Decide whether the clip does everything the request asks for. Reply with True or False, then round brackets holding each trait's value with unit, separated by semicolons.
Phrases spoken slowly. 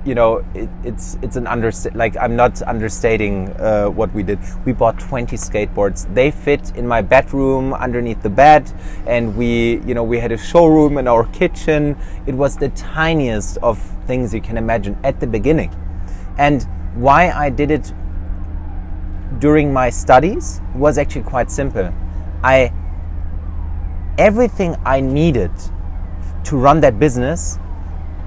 False (145 wpm)